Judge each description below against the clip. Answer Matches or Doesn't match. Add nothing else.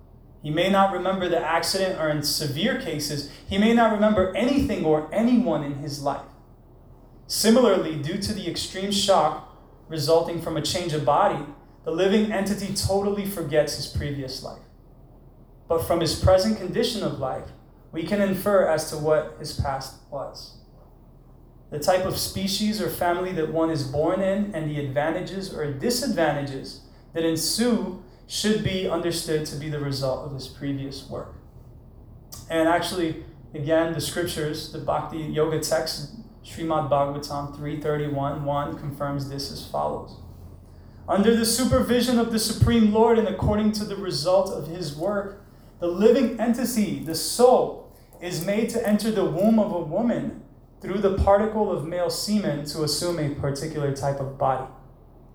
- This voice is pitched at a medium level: Matches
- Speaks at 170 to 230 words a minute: Doesn't match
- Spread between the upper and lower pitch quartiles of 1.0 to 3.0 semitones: Doesn't match